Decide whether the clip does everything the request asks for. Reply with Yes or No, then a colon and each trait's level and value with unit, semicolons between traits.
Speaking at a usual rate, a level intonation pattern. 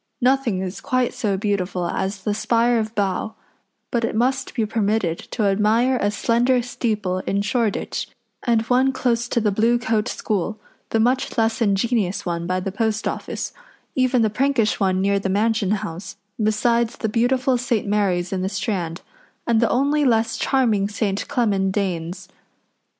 No: average, 165 wpm; average, 3.4 semitones